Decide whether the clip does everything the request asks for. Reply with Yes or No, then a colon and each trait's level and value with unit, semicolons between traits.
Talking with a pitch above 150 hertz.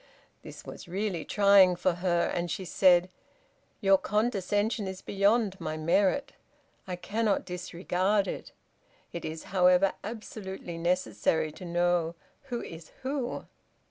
Yes: medium, 185 Hz